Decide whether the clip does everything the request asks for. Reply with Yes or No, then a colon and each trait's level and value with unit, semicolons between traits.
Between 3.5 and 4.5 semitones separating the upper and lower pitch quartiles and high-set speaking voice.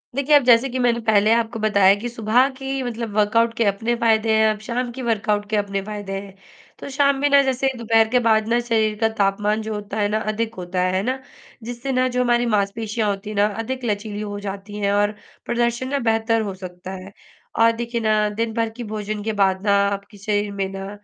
No: narrow, 2.5 semitones; high, 220 Hz